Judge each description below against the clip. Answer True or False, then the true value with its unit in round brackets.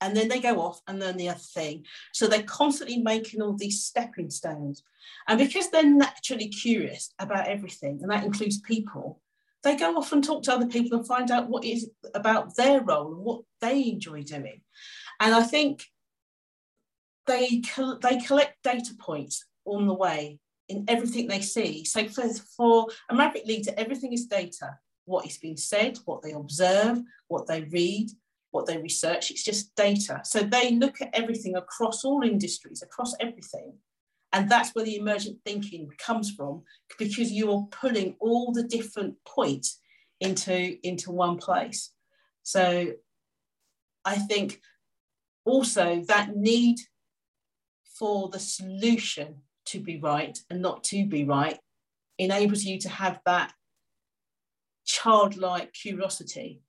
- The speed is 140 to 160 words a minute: True (150 wpm)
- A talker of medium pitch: False (210 Hz)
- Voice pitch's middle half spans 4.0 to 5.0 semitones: True (4.5 semitones)